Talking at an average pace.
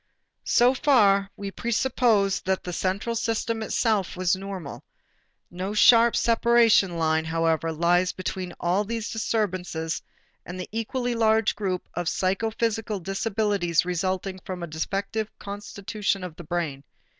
No: slow, 130 wpm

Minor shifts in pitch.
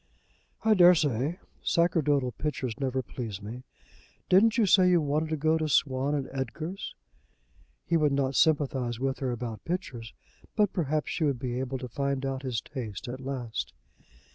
No: average, 3.9 semitones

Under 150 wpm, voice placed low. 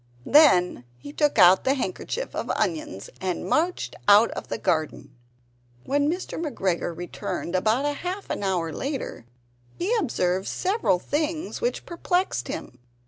No: average, 140 wpm; high, 230 Hz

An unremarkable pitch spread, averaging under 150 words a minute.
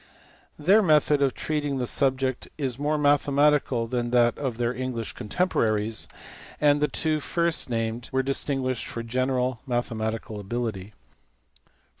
Yes: average, 3.8 semitones; slow, 135 wpm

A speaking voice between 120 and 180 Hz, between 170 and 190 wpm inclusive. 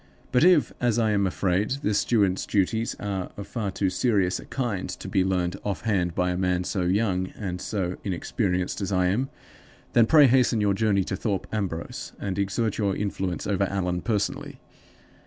No: low, 100 Hz; average, 185 wpm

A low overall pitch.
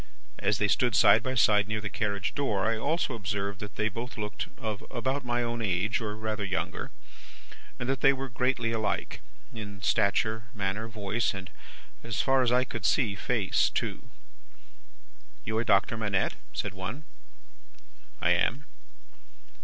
Yes: low, 110 Hz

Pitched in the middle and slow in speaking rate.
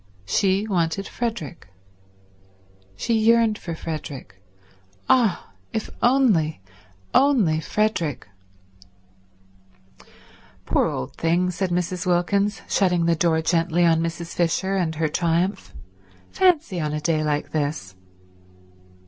Yes: medium, 175 Hz; slow, 105 wpm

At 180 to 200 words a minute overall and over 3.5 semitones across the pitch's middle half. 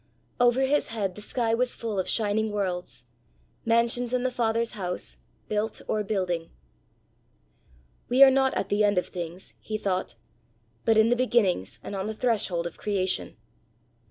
No: average, 165 wpm; average, 4.1 semitones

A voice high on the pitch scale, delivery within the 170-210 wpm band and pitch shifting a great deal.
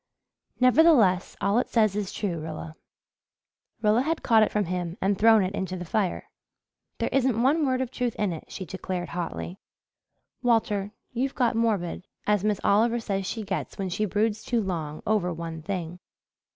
No: high, 205 Hz; average, 175 wpm; average, 4.0 semitones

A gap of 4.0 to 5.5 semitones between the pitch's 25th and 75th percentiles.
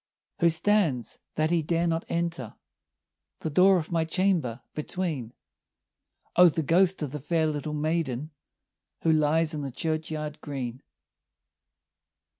No: narrow, 2.4 semitones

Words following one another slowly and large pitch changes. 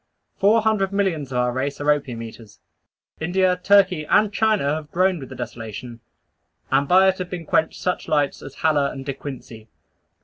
No: average, 180 wpm; wide, 6.1 semitones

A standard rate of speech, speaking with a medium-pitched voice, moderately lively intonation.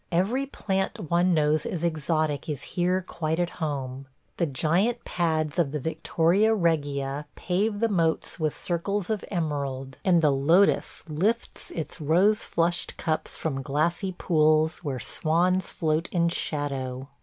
Yes: average, 145 wpm; medium, 165 Hz; average, 3.4 semitones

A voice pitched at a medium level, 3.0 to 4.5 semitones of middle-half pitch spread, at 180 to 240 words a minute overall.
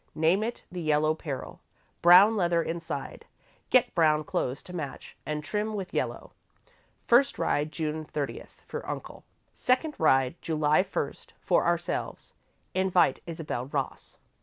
No: medium, 165 Hz; average, 3.7 semitones; slow, 135 wpm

